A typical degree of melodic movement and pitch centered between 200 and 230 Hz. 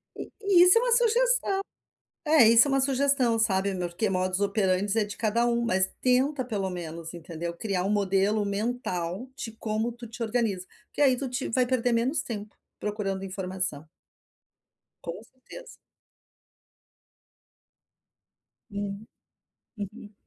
Yes: average, 4.6 semitones; high, 215 Hz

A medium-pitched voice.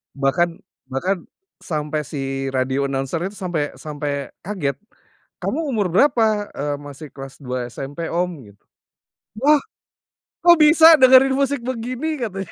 Yes: medium, 170 Hz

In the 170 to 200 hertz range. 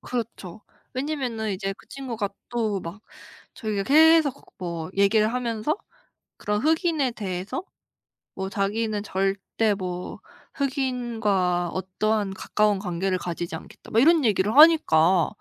No: high, 215 Hz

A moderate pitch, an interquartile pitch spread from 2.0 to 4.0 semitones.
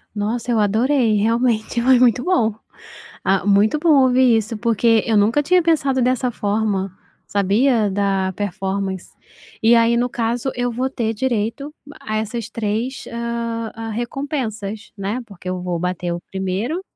No: high, 225 Hz; average, 3.4 semitones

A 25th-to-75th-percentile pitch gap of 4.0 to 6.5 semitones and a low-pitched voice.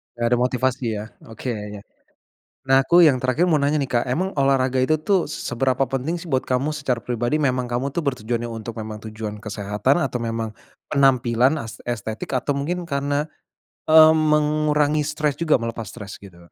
Yes: average, 4.3 semitones; low, 130 Hz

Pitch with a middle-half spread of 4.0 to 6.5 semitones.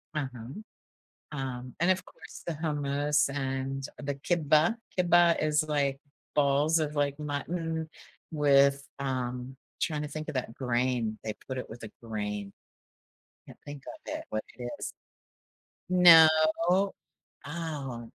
No: average, 3.3 semitones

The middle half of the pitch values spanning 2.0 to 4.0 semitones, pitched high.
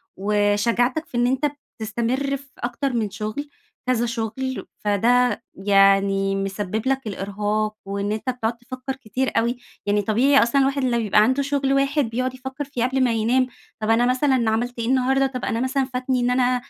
Yes: average, 3.5 semitones; high, 245 Hz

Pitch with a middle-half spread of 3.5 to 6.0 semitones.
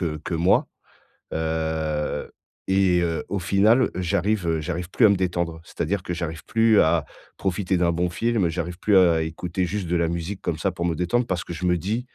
No: average, 2.9 semitones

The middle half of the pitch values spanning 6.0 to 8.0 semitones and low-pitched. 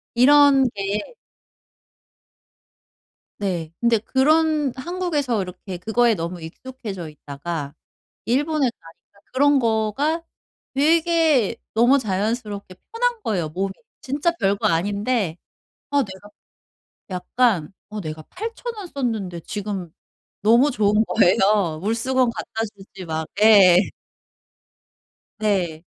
No: wide, 6.5 semitones; high, 215 Hz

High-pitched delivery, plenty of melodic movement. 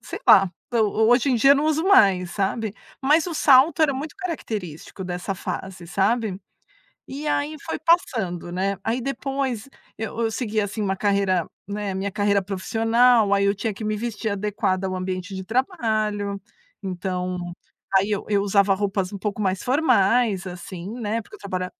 No: high, 205 Hz; average, 4.0 semitones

